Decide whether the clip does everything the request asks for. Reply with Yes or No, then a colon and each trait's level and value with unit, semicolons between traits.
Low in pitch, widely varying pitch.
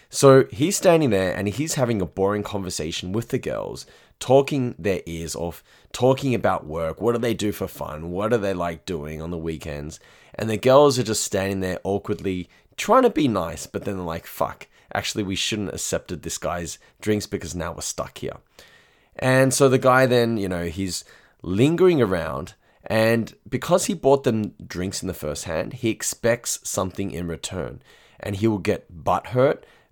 Yes: low, 100 Hz; wide, 5.9 semitones